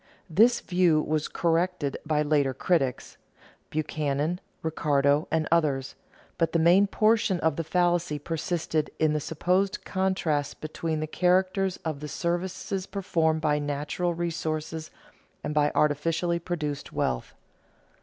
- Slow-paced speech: Yes, slow, 125 wpm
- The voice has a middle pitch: Yes, medium, 160 Hz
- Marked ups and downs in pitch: No, average, 2.9 semitones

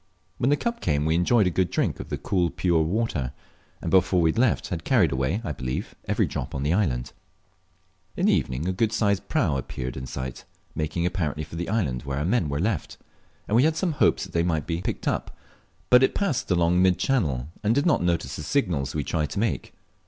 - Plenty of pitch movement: Yes, wide, 6.4 semitones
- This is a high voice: No, very low, 85 Hz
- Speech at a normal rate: No, fast, 225 wpm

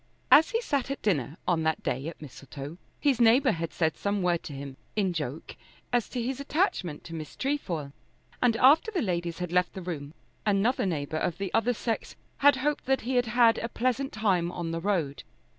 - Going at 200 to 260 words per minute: Yes, fast, 205 wpm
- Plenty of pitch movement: Yes, wide, 7.5 semitones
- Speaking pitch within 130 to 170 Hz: No, high, 195 Hz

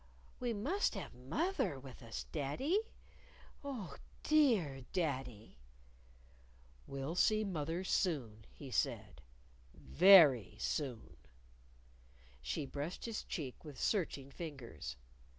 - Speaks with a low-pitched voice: No, medium, 145 Hz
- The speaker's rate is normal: No, slow, 105 wpm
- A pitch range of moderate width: No, wide, 7.7 semitones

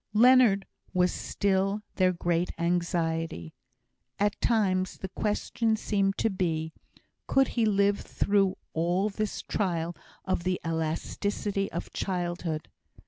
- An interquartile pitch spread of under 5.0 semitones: Yes, average, 3.0 semitones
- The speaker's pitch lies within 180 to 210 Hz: Yes, high, 190 Hz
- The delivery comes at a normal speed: No, slow, 115 wpm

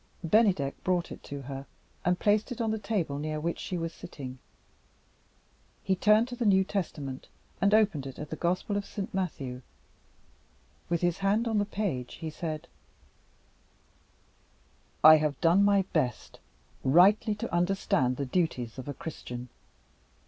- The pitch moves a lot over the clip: Yes, wide, 6.0 semitones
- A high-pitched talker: No, medium, 175 Hz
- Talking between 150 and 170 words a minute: Yes, average, 155 wpm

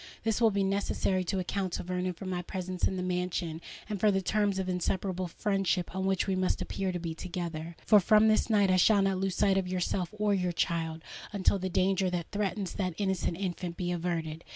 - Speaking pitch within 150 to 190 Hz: Yes, medium, 185 Hz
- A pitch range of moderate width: No, narrow, 1.8 semitones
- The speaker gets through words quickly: Yes, fast, 220 wpm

